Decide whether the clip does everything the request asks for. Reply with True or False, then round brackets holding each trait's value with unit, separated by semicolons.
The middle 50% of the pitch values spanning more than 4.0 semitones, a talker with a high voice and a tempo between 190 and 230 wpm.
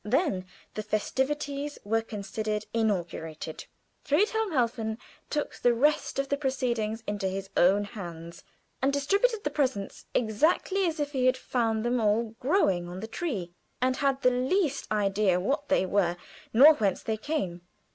False (5.6 semitones; 230 Hz; 155 wpm)